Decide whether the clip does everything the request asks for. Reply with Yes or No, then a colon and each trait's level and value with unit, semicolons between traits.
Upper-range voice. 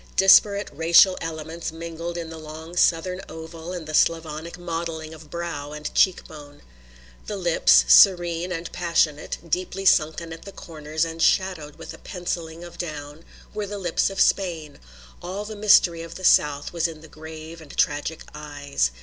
No: medium, 165 Hz